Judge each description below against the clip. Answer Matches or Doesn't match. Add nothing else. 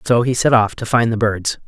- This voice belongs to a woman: Doesn't match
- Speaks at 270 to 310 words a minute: Matches